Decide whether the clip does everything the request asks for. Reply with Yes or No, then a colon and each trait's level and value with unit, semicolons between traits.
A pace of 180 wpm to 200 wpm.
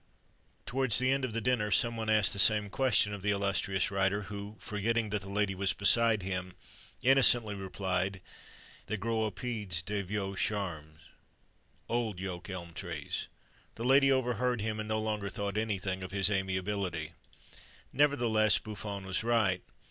No: average, 160 wpm